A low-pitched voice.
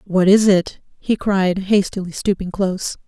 No: high, 190 Hz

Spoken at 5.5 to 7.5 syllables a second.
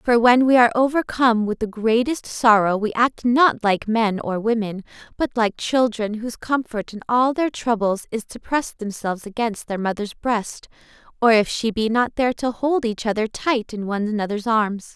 No: 5.0 syllables/s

